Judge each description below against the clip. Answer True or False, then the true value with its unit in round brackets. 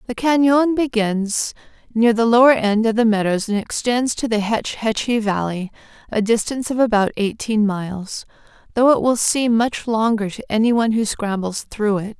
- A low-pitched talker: False (225 Hz)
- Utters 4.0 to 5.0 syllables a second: True (4.9 syllables/s)